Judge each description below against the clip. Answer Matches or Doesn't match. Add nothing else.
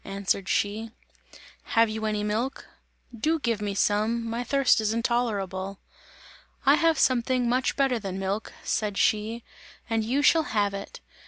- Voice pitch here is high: Matches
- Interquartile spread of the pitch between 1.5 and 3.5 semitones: Matches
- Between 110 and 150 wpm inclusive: Matches